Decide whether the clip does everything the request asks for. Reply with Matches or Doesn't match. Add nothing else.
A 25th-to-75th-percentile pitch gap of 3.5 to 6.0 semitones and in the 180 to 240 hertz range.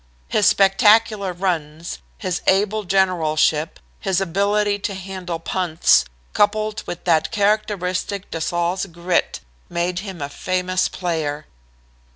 Doesn't match